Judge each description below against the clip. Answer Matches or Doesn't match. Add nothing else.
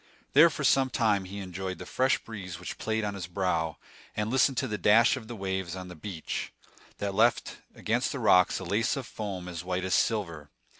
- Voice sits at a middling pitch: Doesn't match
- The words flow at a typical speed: Doesn't match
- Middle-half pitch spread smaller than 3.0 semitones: Doesn't match